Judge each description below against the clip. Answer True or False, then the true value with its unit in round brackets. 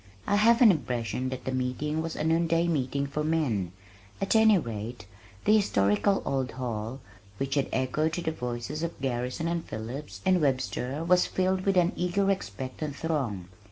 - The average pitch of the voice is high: False (145 Hz)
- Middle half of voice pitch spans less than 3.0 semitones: False (5.3 semitones)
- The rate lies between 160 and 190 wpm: True (175 wpm)